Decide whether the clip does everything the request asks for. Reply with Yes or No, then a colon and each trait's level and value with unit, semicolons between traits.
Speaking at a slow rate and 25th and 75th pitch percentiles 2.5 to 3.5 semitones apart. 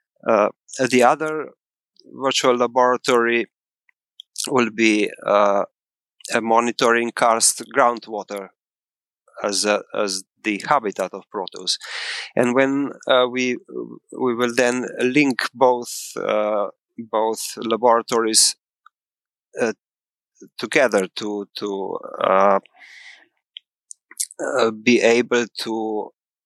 Yes: slow, 90 wpm; average, 2.9 semitones